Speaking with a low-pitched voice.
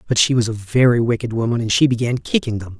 Yes: low, 120 Hz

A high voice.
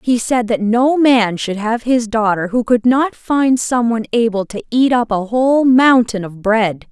Yes: high, 235 Hz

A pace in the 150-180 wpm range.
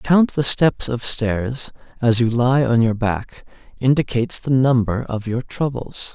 Yes: average, 175 wpm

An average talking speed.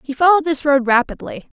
Yes: average, 190 wpm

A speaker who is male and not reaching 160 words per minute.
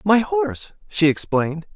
Yes: male; slow, 135 wpm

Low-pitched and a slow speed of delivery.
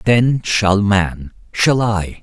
Yes: low, 105 Hz; slow, 110 wpm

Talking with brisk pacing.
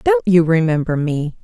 No: average, 165 wpm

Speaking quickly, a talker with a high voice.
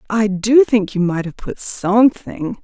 No: average, 180 wpm; high, 210 Hz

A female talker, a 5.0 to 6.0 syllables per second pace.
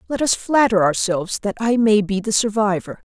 Yes: female; 5.3 syllables/s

